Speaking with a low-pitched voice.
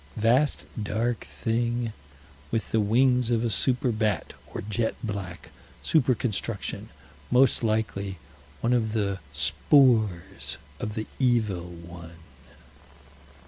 Yes: low, 110 Hz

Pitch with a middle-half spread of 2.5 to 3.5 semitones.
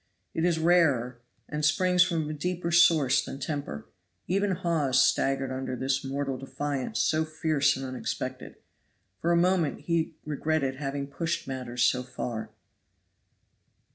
No: average, 4.0 semitones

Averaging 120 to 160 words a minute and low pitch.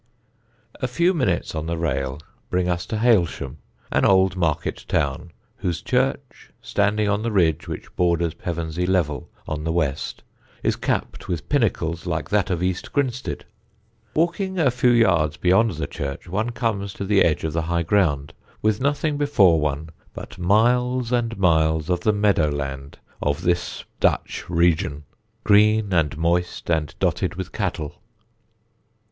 Yes: average, 155 wpm; very low, 90 Hz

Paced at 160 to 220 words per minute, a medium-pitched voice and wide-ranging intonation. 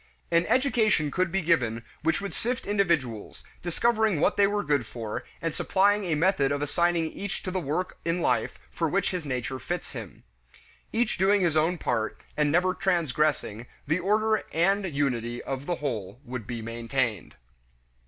Yes: average, 170 wpm; medium, 165 Hz; wide, 6.6 semitones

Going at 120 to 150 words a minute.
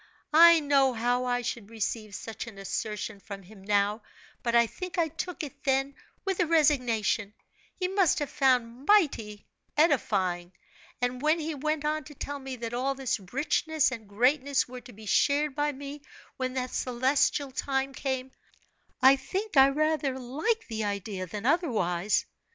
No: average, 165 wpm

